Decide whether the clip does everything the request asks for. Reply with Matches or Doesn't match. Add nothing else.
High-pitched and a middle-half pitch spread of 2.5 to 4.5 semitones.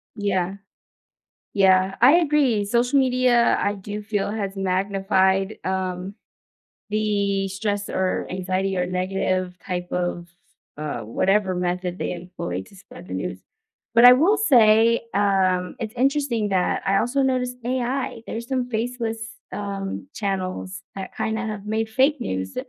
Matches